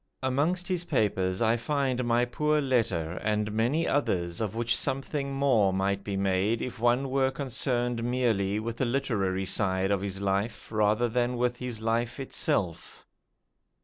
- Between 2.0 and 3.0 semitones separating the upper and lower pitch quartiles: No, average, 4.6 semitones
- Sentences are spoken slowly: No, average, 155 wpm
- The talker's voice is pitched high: No, low, 115 Hz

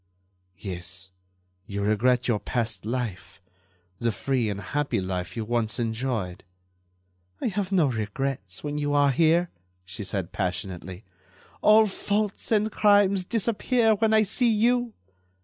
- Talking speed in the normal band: No, slow, 130 wpm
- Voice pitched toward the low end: Yes, low, 120 Hz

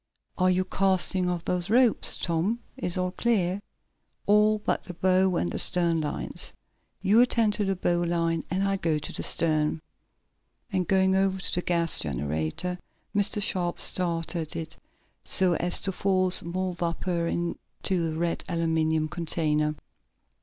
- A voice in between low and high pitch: Yes, medium, 180 Hz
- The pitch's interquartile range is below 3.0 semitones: Yes, narrow, 2.4 semitones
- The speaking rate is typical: Yes, average, 150 wpm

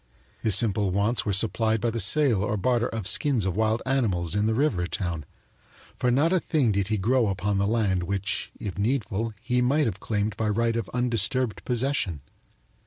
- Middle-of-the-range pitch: No, low, 110 Hz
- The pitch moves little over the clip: No, average, 3.7 semitones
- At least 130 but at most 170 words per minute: No, average, 190 wpm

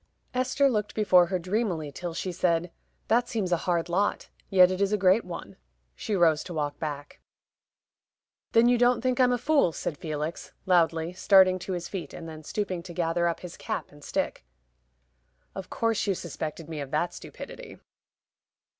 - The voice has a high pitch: No, medium, 180 Hz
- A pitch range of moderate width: Yes, average, 3.9 semitones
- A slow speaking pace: No, average, 180 wpm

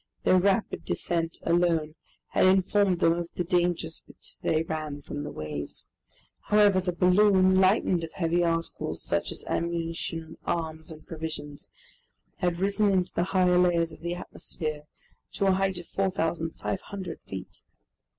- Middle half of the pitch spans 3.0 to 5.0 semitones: No, narrow, 2.5 semitones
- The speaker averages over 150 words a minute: No, average, 145 wpm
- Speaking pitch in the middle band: Yes, medium, 170 Hz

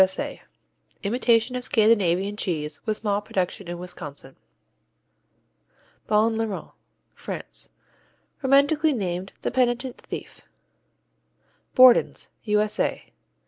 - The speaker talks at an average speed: No, slow, 90 wpm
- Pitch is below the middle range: No, high, 210 Hz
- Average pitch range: Yes, average, 4.9 semitones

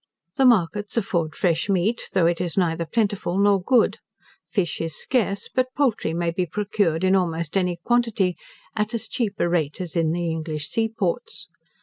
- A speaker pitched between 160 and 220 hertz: Yes, medium, 185 Hz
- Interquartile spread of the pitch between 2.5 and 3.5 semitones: No, average, 4.1 semitones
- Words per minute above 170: Yes, average, 180 wpm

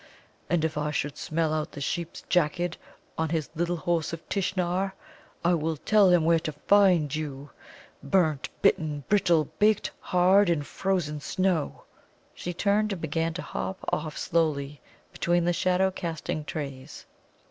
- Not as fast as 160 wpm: Yes, average, 150 wpm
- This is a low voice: No, medium, 165 Hz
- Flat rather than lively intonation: No, average, 3.0 semitones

